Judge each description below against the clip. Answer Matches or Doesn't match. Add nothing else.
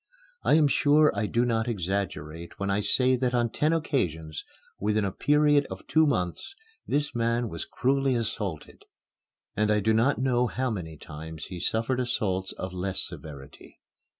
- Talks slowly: Doesn't match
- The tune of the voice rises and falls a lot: Matches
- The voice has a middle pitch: Doesn't match